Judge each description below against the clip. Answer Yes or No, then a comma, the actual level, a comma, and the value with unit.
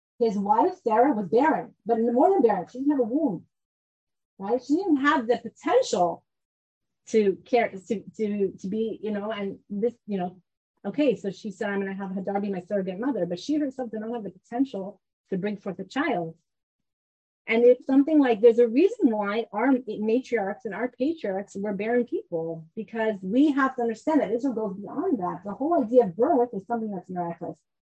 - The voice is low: No, high, 220 Hz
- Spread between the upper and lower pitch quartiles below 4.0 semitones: No, average, 4.3 semitones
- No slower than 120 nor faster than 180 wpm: No, average, 200 wpm